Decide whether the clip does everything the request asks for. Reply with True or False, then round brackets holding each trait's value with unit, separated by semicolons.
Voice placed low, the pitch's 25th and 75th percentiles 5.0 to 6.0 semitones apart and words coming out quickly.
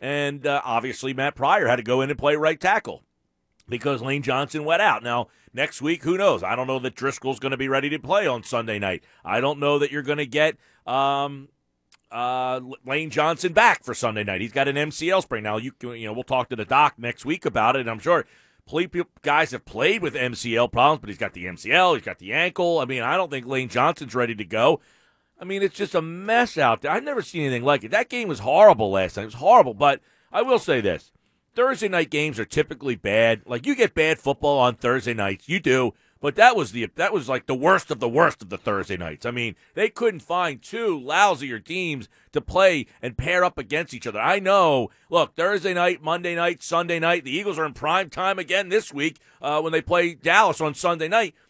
False (145 Hz; 5.4 semitones; 240 wpm)